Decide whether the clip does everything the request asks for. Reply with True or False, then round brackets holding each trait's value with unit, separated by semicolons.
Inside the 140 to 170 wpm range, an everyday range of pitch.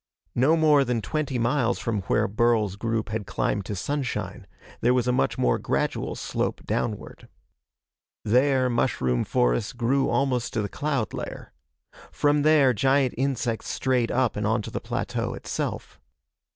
True (150 wpm; 3.9 semitones)